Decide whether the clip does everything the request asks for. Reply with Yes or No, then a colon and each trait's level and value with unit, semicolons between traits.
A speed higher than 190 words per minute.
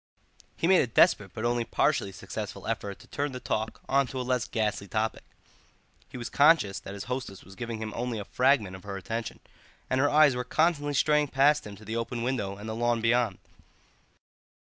Yes: fast, 205 wpm